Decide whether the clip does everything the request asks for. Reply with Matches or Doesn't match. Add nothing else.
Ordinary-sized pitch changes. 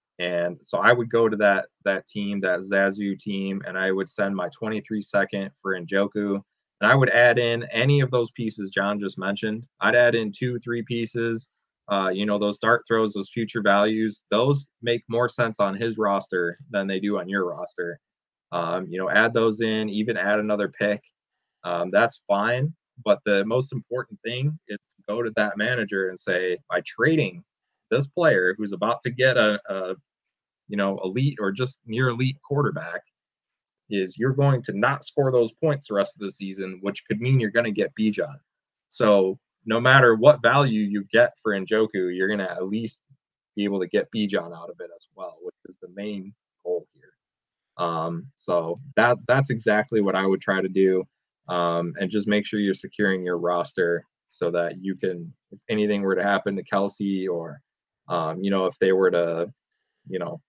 Matches